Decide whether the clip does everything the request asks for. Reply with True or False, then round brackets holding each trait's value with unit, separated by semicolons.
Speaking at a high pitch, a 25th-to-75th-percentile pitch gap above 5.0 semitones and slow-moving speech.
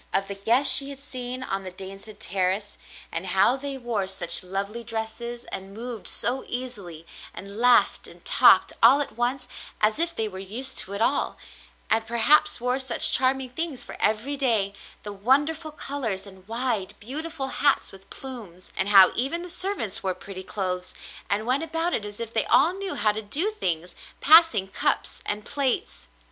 False (230 Hz; 5.5 semitones; 180 wpm)